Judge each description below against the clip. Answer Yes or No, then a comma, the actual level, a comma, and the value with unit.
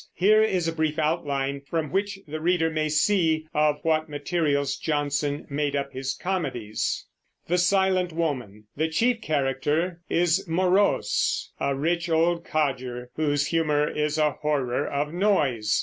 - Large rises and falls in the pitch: No, average, 3.3 semitones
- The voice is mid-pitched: Yes, medium, 155 Hz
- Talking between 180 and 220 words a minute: No, slow, 135 wpm